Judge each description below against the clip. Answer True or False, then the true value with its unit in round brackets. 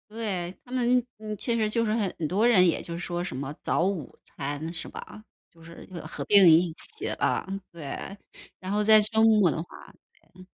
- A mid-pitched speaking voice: False (195 Hz)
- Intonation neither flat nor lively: True (4.3 semitones)